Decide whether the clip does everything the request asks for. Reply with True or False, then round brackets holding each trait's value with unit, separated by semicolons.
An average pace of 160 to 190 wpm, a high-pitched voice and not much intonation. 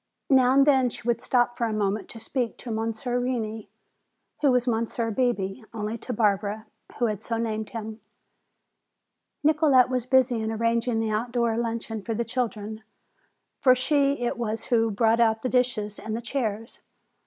True (170 wpm; 230 Hz; 2.2 semitones)